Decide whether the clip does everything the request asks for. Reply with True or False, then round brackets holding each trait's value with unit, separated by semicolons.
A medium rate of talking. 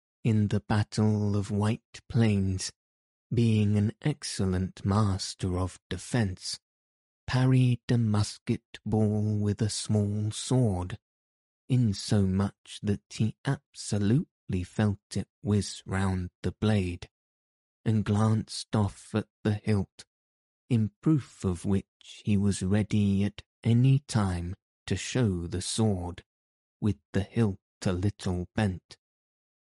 False (115 wpm)